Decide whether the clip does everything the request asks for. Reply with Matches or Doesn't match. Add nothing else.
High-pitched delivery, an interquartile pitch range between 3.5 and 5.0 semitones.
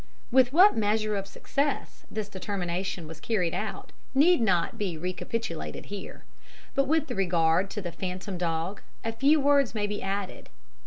Matches